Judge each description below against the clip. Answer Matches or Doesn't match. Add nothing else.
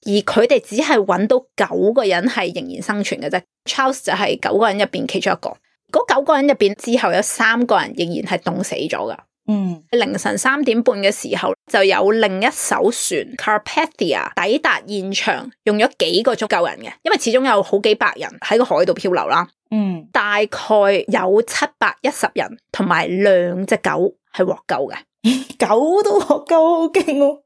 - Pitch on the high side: Matches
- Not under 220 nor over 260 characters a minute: Doesn't match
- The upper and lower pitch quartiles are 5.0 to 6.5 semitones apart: Matches